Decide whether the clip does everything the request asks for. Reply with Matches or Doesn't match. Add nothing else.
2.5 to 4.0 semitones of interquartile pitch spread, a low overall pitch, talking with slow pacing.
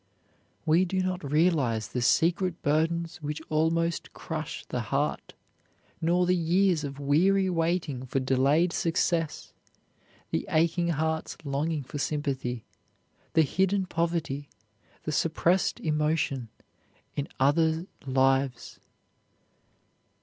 Doesn't match